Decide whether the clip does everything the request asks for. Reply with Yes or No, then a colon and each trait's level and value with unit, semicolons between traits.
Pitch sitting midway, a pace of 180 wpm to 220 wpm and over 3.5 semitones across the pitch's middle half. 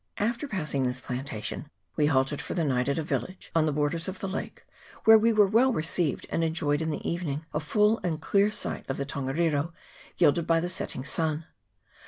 Yes: medium, 160 Hz; fast, 205 wpm; average, 4.3 semitones